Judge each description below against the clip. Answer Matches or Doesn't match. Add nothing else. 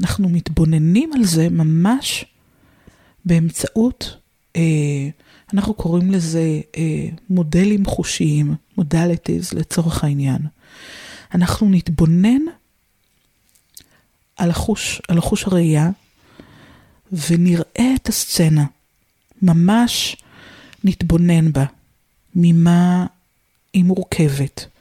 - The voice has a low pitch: Doesn't match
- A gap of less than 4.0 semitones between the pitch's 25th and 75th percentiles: Matches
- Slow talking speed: Matches